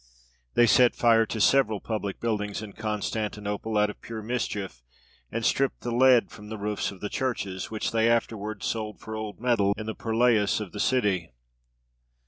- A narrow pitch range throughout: Yes, narrow, 2.0 semitones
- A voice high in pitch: No, low, 110 Hz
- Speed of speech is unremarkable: Yes, average, 175 wpm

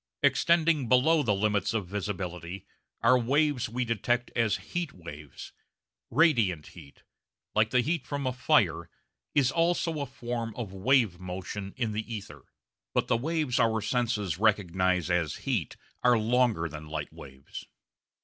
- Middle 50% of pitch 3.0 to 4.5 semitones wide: No, wide, 5.5 semitones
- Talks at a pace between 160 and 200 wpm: No, average, 145 wpm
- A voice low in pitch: Yes, low, 115 Hz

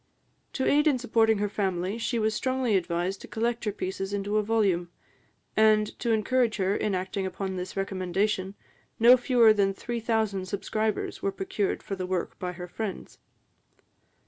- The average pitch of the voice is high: Yes, high, 205 Hz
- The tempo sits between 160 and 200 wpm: Yes, average, 170 wpm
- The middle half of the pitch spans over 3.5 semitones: No, average, 2.9 semitones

